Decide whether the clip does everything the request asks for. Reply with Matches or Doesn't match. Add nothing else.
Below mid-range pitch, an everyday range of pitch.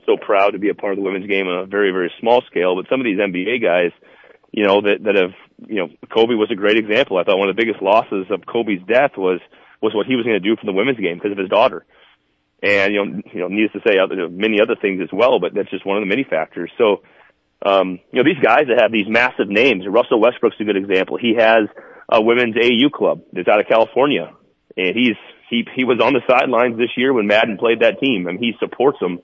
Matches